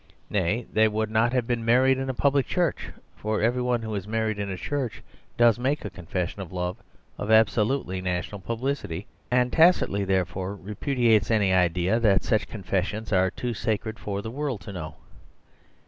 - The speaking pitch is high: No, low, 110 Hz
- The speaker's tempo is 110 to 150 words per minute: No, average, 180 wpm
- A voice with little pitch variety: No, average, 4.1 semitones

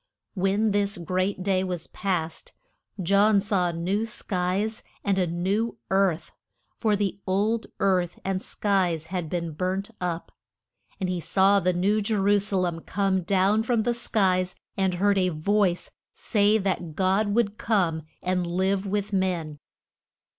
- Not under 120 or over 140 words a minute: No, average, 150 wpm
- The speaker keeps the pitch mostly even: Yes, narrow, 2.2 semitones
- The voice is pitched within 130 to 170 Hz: No, high, 190 Hz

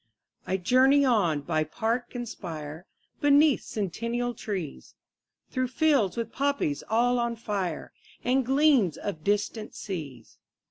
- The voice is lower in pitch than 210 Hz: No, high, 225 Hz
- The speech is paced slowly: Yes, slow, 130 wpm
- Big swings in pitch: Yes, wide, 6.2 semitones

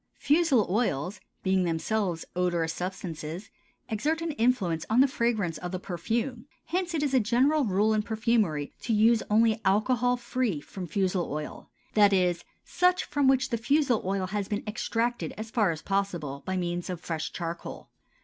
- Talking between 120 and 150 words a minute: No, average, 170 wpm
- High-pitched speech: Yes, high, 210 Hz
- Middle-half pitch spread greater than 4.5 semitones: Yes, average, 5.3 semitones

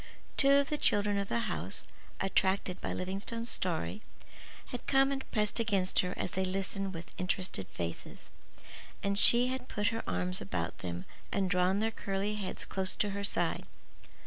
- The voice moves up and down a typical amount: Yes, average, 3.3 semitones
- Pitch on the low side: No, high, 195 Hz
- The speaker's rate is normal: Yes, average, 170 wpm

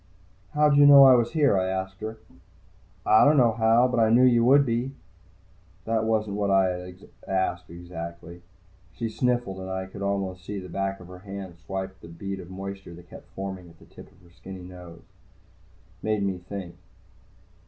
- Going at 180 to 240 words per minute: Yes, average, 195 wpm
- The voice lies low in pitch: Yes, very low, 95 Hz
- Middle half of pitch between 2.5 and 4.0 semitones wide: Yes, average, 3.6 semitones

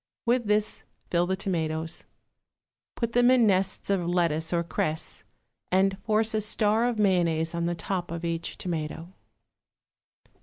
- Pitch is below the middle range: No, medium, 185 Hz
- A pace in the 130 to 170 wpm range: Yes, average, 145 wpm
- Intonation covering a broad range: No, average, 4.1 semitones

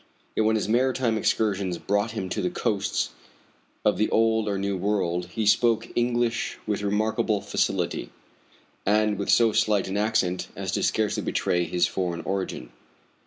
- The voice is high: No, low, 105 Hz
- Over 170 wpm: No, average, 160 wpm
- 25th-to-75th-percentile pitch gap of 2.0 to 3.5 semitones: Yes, narrow, 2.6 semitones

